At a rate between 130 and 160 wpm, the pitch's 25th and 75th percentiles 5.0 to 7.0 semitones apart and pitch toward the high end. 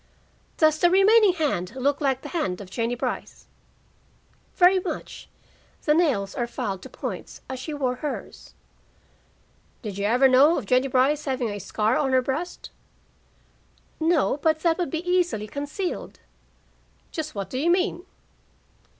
Yes: average, 150 wpm; average, 5.3 semitones; very high, 280 Hz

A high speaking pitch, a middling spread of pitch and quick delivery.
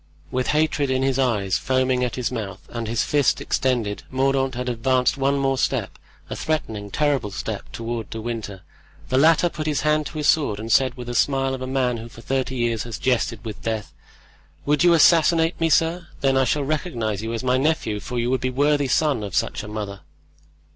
No: low, 130 Hz; average, 3.9 semitones; fast, 215 wpm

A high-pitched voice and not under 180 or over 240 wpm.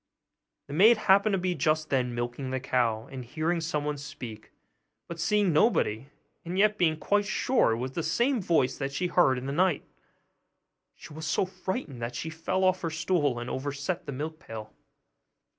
No: medium, 155 Hz; average, 190 wpm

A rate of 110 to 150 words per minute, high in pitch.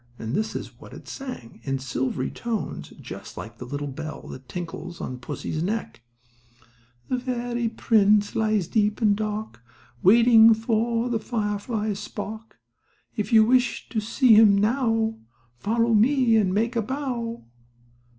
Yes: average, 145 wpm; high, 220 Hz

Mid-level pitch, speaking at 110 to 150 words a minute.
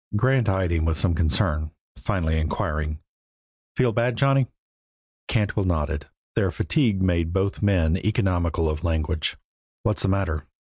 No: very low, 90 Hz; slow, 135 wpm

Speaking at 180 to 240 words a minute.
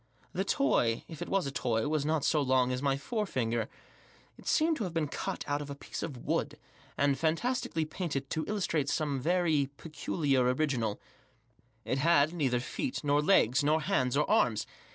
Yes: average, 185 wpm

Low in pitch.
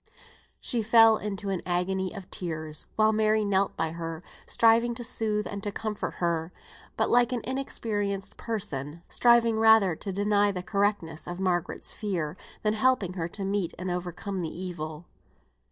No: high, 200 Hz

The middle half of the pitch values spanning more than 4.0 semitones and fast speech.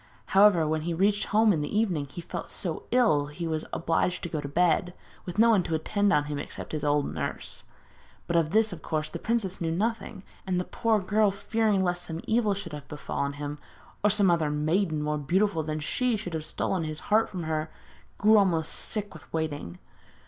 Yes: average, 4.9 semitones; fast, 210 wpm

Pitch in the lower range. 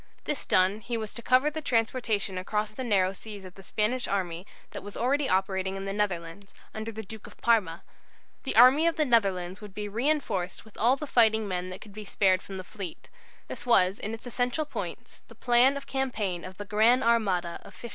No: high, 215 Hz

